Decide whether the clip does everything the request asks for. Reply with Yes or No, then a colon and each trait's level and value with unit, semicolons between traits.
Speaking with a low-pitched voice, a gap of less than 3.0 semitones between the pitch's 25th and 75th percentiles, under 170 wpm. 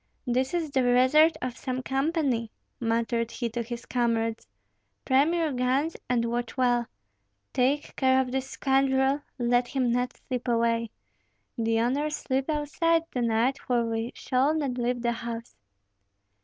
No: very high, 250 Hz; narrow, 2.4 semitones; average, 150 wpm